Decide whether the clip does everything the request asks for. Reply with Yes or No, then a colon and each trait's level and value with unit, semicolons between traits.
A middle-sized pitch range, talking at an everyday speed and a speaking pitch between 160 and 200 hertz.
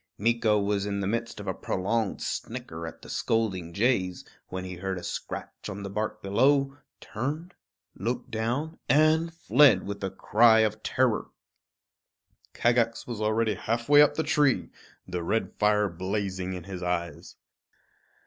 No: average, 4.0 semitones; average, 150 wpm; low, 105 Hz